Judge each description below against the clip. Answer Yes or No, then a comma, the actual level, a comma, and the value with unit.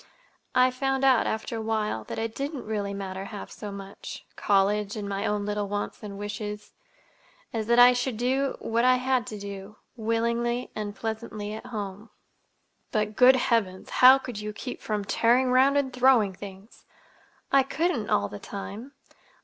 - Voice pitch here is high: Yes, high, 220 Hz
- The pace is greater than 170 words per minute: No, average, 160 wpm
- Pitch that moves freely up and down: No, average, 3.5 semitones